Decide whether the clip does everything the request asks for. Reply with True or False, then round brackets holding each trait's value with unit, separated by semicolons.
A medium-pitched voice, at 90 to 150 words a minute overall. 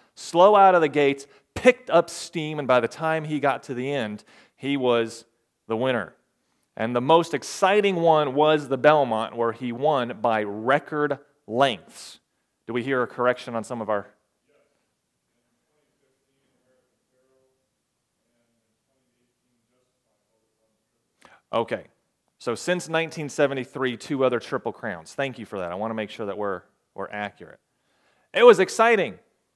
False (130 Hz; 140 wpm)